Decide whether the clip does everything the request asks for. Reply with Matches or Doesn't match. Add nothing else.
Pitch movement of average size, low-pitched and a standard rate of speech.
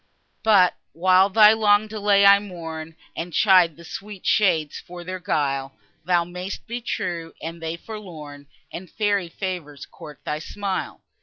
Doesn't match